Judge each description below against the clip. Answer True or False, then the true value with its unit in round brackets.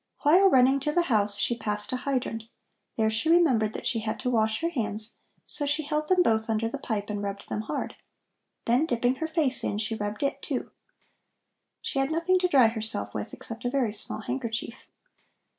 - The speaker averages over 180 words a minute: True (200 wpm)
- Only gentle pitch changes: False (4.9 semitones)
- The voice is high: True (240 Hz)